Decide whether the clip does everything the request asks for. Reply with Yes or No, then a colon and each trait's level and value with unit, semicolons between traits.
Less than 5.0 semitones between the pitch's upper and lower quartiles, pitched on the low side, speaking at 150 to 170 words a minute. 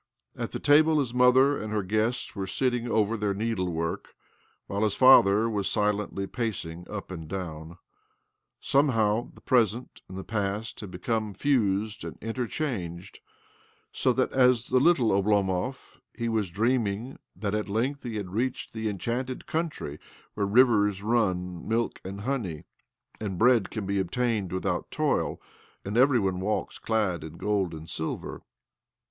Yes: average, 4.0 semitones; low, 105 Hz; average, 155 wpm